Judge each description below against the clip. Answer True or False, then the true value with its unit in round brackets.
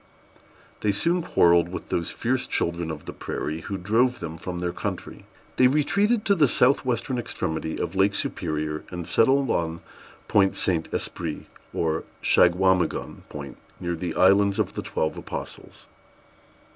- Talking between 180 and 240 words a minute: False (150 wpm)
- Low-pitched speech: True (95 Hz)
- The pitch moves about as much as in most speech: False (6.6 semitones)